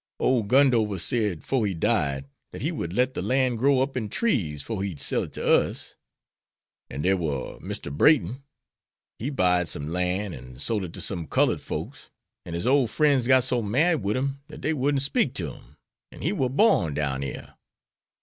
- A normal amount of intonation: No, wide, 7.7 semitones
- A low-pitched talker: Yes, low, 110 Hz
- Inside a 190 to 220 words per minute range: Yes, average, 195 wpm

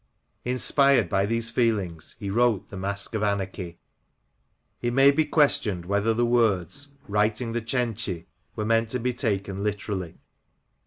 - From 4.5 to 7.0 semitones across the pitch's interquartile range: No, average, 3.5 semitones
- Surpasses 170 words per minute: No, average, 155 wpm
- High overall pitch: No, low, 110 Hz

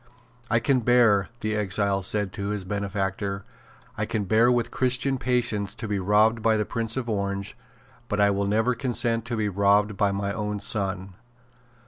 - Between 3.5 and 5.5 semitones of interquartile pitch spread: No, narrow, 2.5 semitones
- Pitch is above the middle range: No, low, 105 Hz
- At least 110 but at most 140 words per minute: No, average, 175 wpm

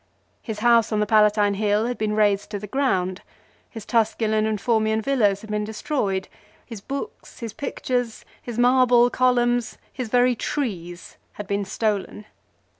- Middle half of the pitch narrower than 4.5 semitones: Yes, average, 2.7 semitones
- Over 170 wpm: No, average, 155 wpm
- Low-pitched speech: No, high, 220 Hz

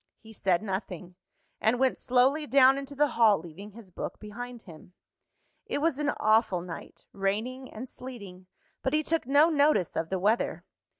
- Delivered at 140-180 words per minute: Yes, average, 170 wpm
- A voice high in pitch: Yes, high, 230 Hz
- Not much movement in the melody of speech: No, wide, 5.5 semitones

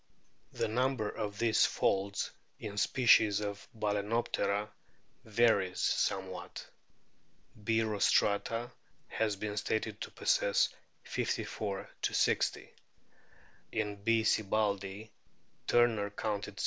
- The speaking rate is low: Yes, slow, 95 wpm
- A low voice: Yes, low, 105 Hz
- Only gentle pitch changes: Yes, narrow, 1.7 semitones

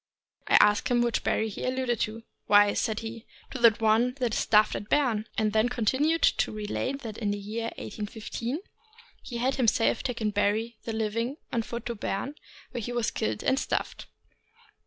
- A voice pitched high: Yes, high, 230 Hz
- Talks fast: Yes, fast, 210 wpm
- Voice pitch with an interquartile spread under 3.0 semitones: Yes, narrow, 2.4 semitones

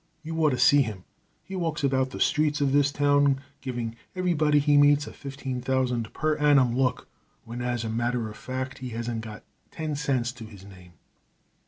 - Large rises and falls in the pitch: No, average, 3.4 semitones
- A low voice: Yes, low, 130 Hz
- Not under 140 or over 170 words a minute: No, average, 190 wpm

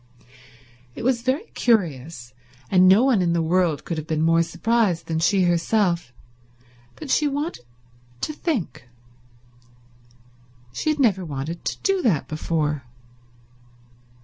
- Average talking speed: No, slow, 130 wpm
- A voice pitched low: No, medium, 175 Hz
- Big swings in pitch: Yes, wide, 6.8 semitones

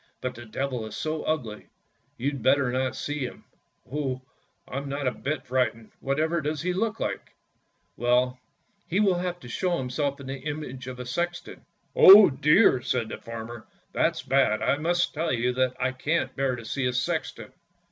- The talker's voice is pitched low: Yes, low, 130 Hz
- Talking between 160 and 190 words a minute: Yes, average, 180 wpm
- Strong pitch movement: No, average, 3.4 semitones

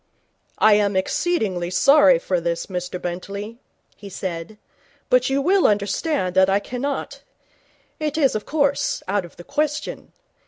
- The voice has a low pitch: No, high, 205 Hz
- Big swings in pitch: Yes, wide, 7.4 semitones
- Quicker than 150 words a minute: No, average, 145 wpm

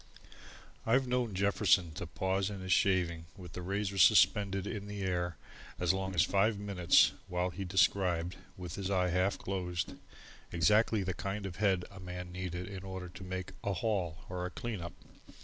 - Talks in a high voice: No, very low, 95 Hz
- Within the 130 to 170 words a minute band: No, average, 185 wpm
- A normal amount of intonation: No, narrow, 1.8 semitones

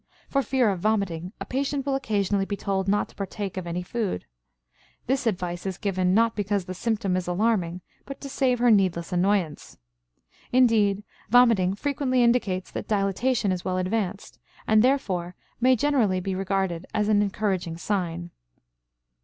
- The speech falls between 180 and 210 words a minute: No, average, 160 wpm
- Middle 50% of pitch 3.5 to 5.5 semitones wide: Yes, average, 4.0 semitones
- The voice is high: Yes, high, 200 Hz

